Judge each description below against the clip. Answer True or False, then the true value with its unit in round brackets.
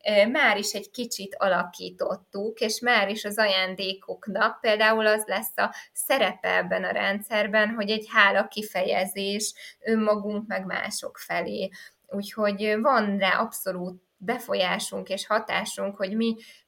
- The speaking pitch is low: False (210 Hz)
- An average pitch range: False (1.7 semitones)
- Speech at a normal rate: True (125 wpm)